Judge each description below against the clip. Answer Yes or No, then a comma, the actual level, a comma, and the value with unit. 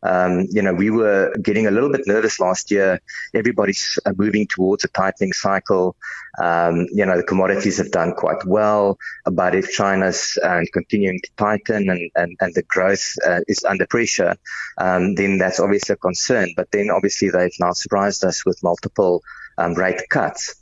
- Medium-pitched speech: No, very low, 95 Hz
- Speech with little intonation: Yes, narrow, 1.8 semitones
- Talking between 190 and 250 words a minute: No, average, 180 wpm